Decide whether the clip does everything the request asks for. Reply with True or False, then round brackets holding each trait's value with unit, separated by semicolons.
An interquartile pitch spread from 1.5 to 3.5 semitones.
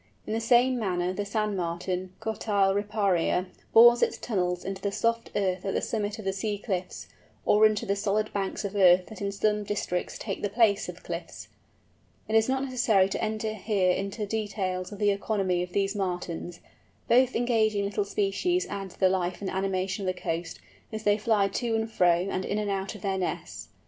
True (2.5 semitones)